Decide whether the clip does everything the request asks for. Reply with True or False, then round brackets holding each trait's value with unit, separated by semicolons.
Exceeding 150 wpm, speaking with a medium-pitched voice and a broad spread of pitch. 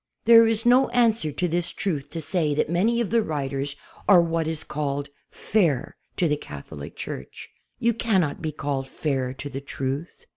True (180 wpm; 160 Hz; 6.8 semitones)